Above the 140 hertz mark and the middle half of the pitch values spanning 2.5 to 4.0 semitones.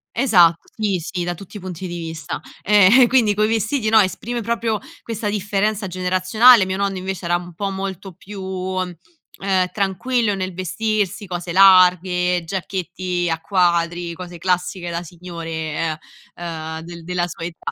Yes: medium, 185 Hz; average, 2.9 semitones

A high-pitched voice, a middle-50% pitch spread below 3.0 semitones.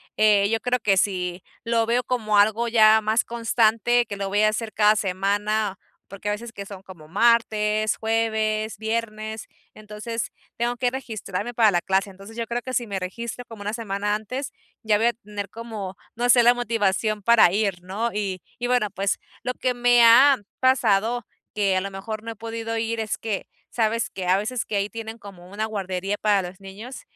Yes: high, 215 Hz; narrow, 2.6 semitones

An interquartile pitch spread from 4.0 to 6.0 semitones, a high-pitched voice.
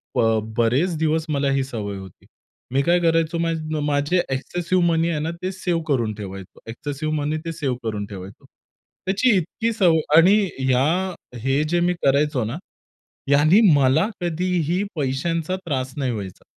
No: average, 4.7 semitones; medium, 150 Hz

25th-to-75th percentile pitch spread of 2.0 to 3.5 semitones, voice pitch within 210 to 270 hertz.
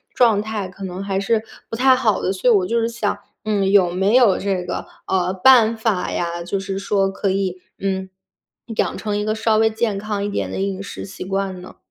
No: narrow, 2.4 semitones; high, 200 Hz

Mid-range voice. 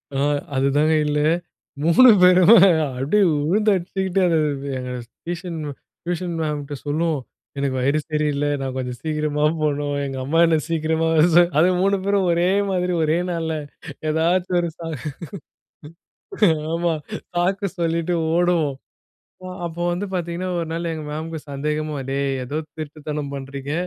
Yes: medium, 160 Hz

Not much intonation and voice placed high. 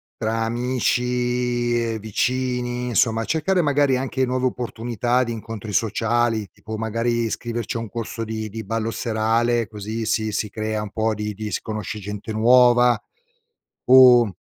No: narrow, 2.0 semitones; low, 115 Hz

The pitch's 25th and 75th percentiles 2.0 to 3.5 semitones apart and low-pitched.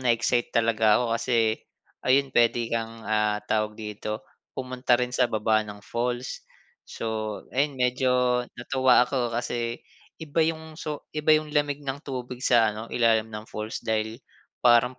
Yes: narrow, 2.5 semitones; low, 120 Hz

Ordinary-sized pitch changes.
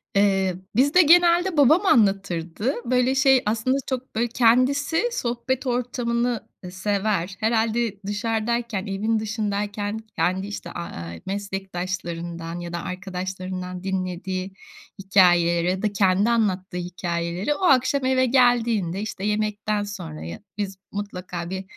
Yes: average, 4.5 semitones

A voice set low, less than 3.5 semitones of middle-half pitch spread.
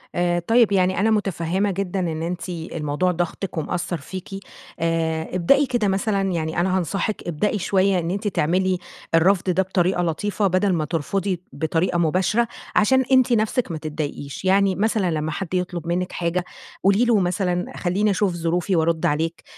No: medium, 180 Hz; average, 2.9 semitones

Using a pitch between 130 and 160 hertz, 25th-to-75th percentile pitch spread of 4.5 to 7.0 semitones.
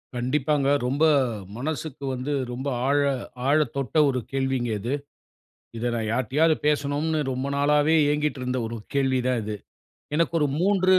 No: medium, 140 Hz; average, 2.9 semitones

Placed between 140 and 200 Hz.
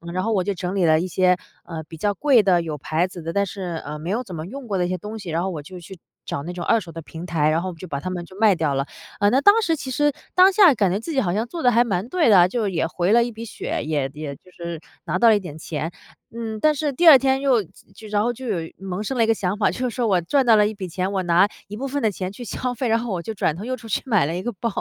Yes: high, 195 Hz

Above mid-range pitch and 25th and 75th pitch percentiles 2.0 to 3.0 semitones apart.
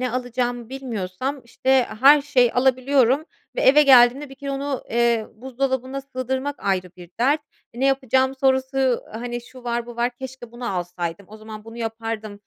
Yes: very high, 250 Hz; narrow, 2.6 semitones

